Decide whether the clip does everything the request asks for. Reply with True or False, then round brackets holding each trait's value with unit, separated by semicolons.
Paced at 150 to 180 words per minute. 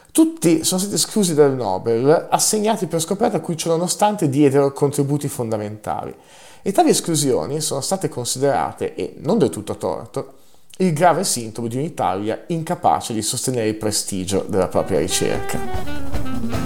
False (140 wpm)